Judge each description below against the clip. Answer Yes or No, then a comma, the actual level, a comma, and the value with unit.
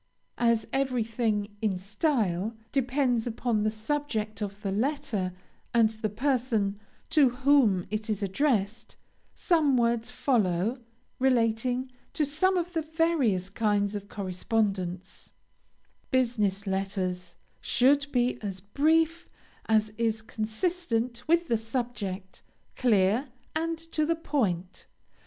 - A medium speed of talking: No, slow, 115 wpm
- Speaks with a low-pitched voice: No, high, 230 Hz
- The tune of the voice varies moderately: Yes, average, 5.0 semitones